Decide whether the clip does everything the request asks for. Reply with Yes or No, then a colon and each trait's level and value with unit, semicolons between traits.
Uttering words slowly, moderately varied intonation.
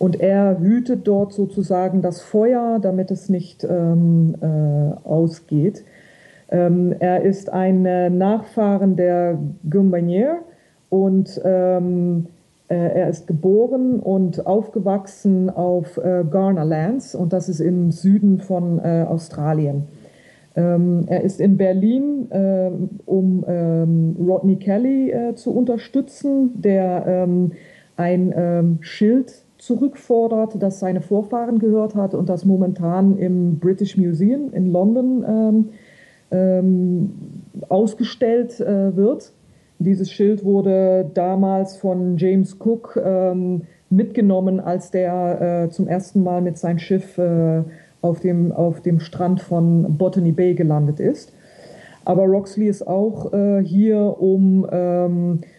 No: slow, 120 wpm; narrow, 2.2 semitones